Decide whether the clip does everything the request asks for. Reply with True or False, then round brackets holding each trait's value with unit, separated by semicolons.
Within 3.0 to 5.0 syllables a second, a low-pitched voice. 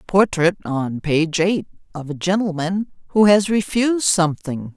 False (4.5 syllables/s; 180 Hz)